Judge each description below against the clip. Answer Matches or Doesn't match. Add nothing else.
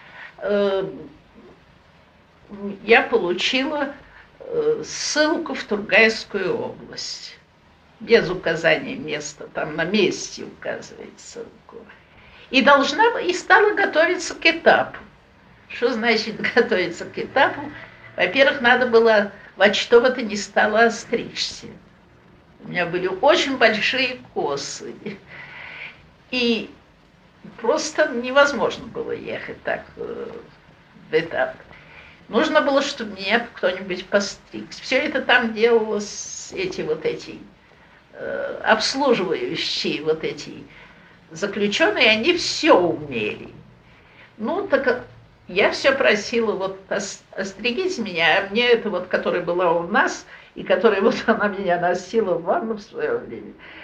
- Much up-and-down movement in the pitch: Matches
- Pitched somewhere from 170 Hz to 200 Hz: Doesn't match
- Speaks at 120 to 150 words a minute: Doesn't match